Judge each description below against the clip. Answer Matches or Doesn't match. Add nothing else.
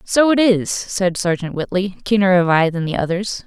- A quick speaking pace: Matches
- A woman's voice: Matches